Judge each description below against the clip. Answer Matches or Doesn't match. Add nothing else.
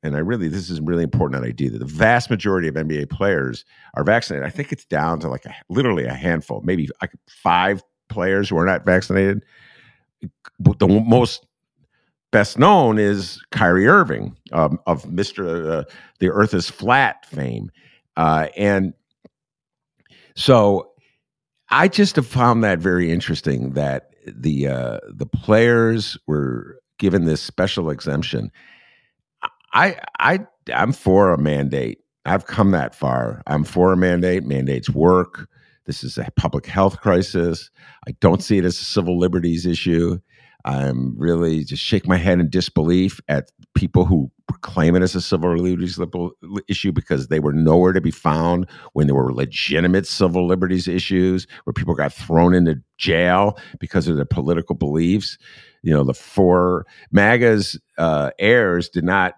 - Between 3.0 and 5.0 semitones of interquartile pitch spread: Matches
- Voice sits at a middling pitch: Doesn't match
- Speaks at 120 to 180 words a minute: Matches